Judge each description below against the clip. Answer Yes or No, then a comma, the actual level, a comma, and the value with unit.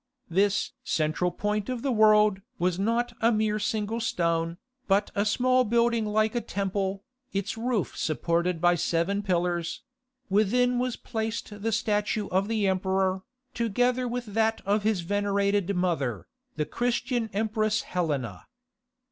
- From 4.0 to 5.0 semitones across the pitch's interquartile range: No, average, 3.4 semitones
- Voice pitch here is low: No, high, 205 Hz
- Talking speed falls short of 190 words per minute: Yes, average, 140 wpm